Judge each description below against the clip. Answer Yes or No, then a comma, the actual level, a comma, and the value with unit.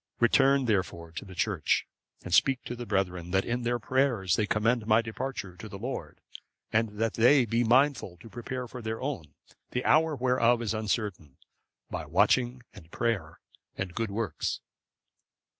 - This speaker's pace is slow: No, average, 165 wpm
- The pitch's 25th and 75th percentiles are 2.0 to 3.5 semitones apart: No, average, 4.4 semitones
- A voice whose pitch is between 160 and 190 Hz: No, low, 115 Hz